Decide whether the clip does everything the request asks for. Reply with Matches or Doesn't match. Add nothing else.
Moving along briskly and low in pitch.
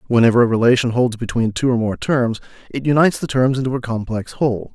Matches